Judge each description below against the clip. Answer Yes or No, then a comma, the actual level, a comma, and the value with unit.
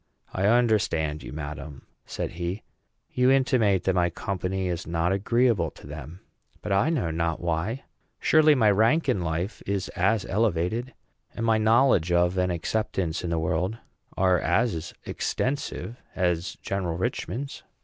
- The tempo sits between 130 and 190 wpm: Yes, average, 150 wpm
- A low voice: Yes, very low, 95 Hz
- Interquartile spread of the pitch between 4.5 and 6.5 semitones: Yes, average, 4.9 semitones